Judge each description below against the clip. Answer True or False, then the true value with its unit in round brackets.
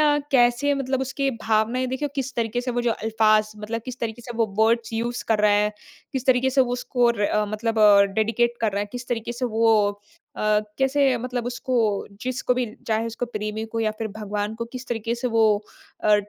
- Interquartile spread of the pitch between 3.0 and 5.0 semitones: False (2.4 semitones)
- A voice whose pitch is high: True (230 Hz)